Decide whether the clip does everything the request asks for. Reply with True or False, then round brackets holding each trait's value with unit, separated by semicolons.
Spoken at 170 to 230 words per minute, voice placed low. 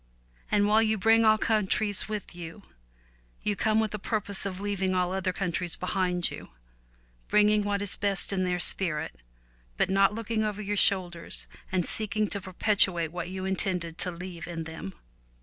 False (175 wpm; 190 Hz)